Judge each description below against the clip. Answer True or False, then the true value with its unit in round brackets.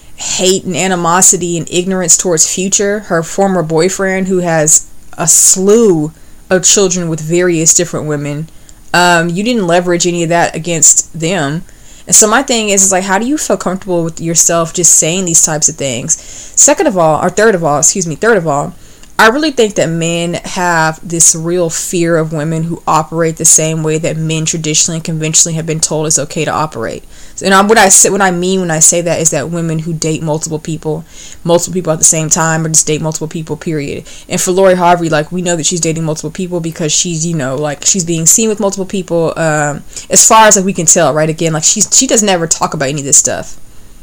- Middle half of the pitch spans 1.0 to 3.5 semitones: True (2.8 semitones)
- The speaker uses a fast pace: True (225 wpm)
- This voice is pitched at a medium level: True (170 Hz)